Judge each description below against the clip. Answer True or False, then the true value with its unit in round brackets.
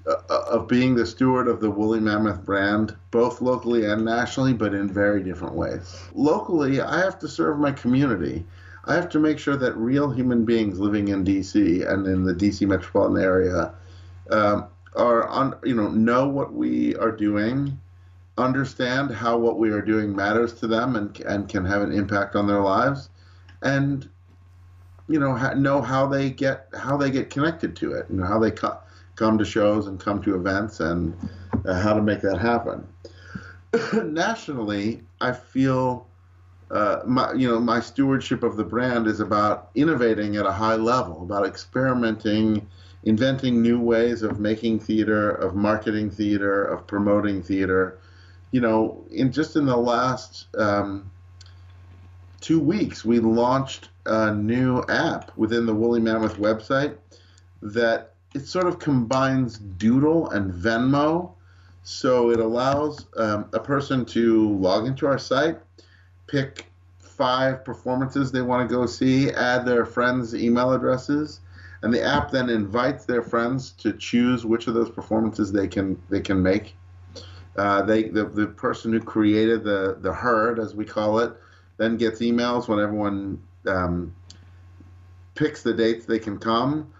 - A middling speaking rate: True (160 wpm)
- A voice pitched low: True (110 Hz)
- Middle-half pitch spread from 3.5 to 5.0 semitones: True (4.5 semitones)